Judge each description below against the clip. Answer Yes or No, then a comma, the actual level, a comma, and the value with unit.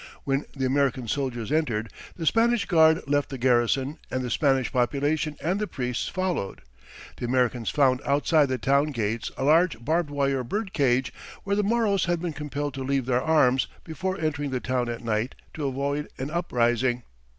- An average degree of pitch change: Yes, average, 4.0 semitones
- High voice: No, medium, 140 Hz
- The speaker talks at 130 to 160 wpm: No, average, 180 wpm